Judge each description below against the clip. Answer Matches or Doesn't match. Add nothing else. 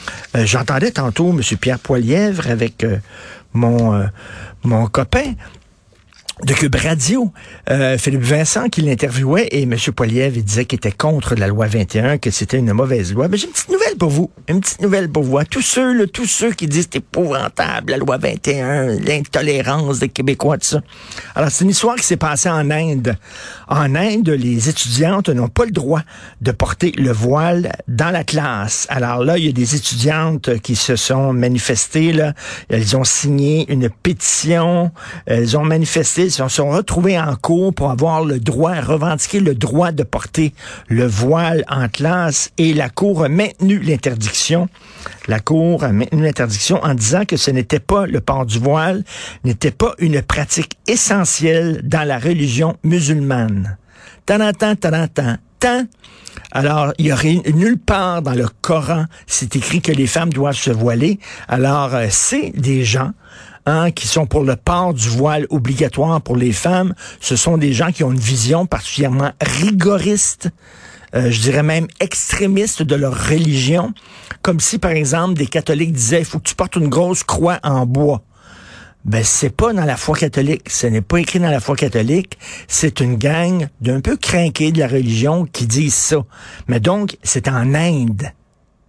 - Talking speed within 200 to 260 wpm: Doesn't match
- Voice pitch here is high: Doesn't match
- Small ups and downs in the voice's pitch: Doesn't match